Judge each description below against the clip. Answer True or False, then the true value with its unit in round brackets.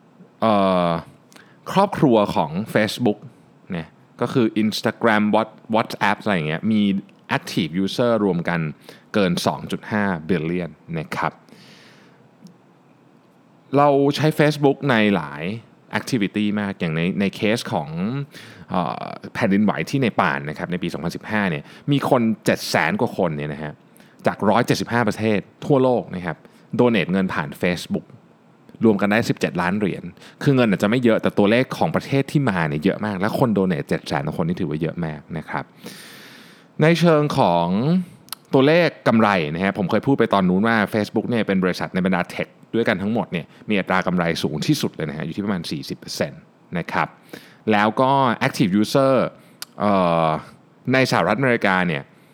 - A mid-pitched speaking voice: False (110 Hz)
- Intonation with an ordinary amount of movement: False (6.7 semitones)